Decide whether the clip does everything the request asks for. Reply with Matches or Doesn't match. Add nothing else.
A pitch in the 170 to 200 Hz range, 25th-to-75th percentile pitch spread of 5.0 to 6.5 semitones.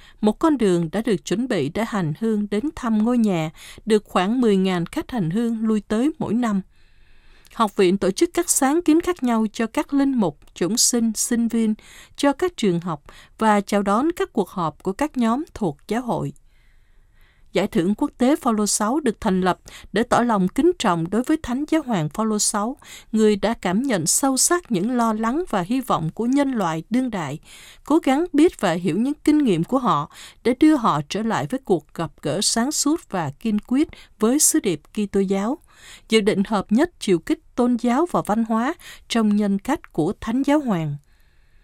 Doesn't match